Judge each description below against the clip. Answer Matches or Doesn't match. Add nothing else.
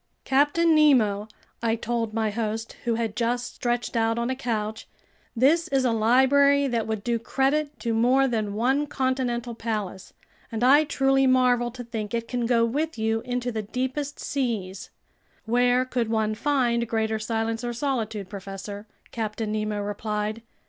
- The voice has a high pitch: Matches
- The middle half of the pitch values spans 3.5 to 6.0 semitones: Doesn't match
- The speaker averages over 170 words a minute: Doesn't match